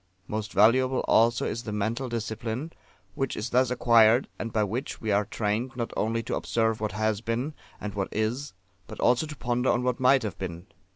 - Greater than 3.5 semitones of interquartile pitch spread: No, narrow, 2.6 semitones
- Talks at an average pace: Yes, average, 195 wpm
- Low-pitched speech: Yes, low, 115 Hz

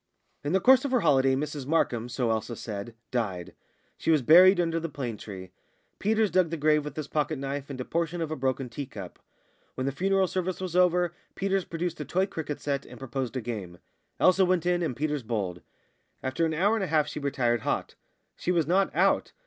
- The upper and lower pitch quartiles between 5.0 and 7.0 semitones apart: Yes, wide, 5.6 semitones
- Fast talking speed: Yes, fast, 215 wpm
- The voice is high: No, medium, 150 Hz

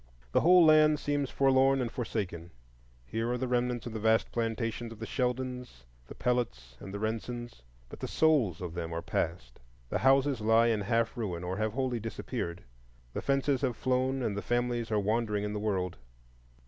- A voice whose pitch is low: Yes, low, 115 Hz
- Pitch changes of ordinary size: Yes, average, 3.7 semitones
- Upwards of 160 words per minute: Yes, average, 185 wpm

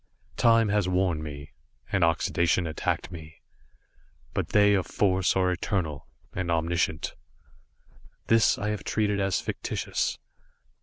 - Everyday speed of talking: No, slow, 120 wpm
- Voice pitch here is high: No, very low, 90 Hz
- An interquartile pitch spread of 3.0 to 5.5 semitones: Yes, average, 3.7 semitones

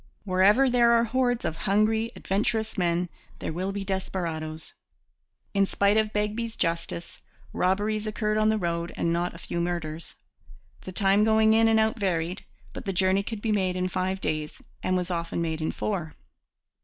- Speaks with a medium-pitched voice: No, high, 195 Hz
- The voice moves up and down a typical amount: Yes, average, 4.0 semitones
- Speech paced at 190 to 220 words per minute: No, average, 175 wpm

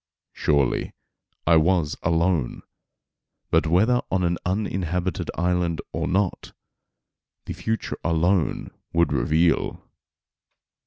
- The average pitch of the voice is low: Yes, very low, 85 Hz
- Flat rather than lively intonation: Yes, narrow, 2.3 semitones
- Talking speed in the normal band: No, slow, 95 wpm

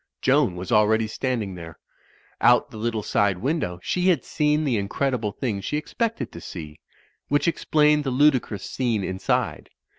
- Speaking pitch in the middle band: No, low, 115 Hz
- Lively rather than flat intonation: Yes, wide, 7.0 semitones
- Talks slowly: No, average, 170 wpm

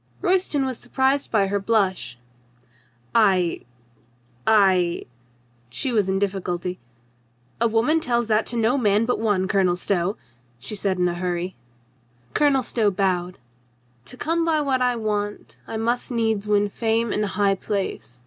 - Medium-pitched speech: No, high, 205 Hz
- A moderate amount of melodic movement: Yes, average, 4.4 semitones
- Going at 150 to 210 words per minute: Yes, average, 160 wpm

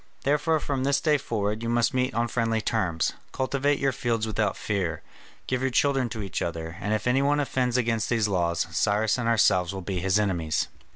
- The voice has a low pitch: Yes, low, 115 Hz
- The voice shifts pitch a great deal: No, average, 4.6 semitones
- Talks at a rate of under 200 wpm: No, fast, 205 wpm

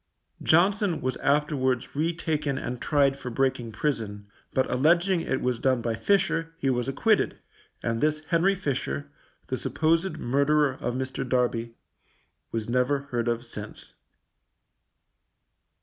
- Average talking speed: No, slow, 130 wpm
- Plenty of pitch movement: No, average, 4.3 semitones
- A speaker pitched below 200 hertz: Yes, low, 135 Hz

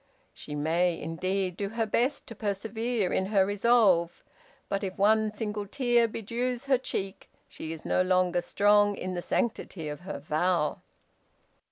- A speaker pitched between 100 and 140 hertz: No, high, 200 Hz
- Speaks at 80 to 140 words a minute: No, average, 155 wpm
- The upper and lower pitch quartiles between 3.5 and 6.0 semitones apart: Yes, average, 3.8 semitones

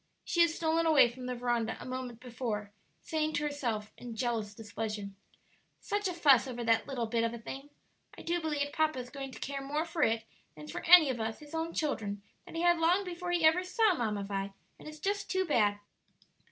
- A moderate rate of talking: No, fast, 220 wpm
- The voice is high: Yes, very high, 270 Hz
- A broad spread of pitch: Yes, wide, 6.1 semitones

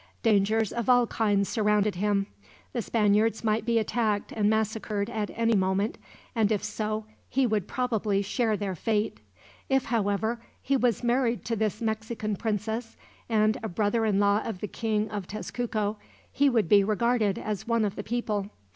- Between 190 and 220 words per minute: No, average, 170 wpm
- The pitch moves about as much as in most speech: No, narrow, 1.9 semitones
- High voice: Yes, high, 215 Hz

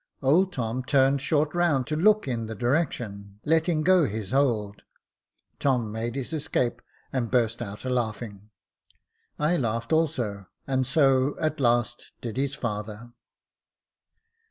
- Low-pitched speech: Yes, low, 130 Hz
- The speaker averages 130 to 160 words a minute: Yes, slow, 135 wpm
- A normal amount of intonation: Yes, average, 4.7 semitones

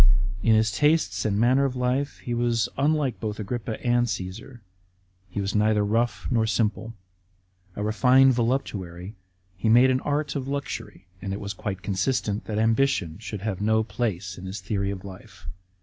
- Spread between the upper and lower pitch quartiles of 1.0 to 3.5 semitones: No, average, 3.9 semitones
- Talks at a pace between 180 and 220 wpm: No, average, 170 wpm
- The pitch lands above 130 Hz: No, low, 110 Hz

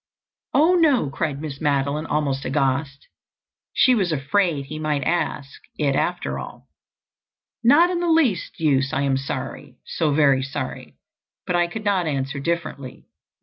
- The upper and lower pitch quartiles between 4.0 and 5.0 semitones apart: Yes, average, 4.5 semitones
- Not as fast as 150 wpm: Yes, average, 140 wpm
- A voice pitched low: No, medium, 150 Hz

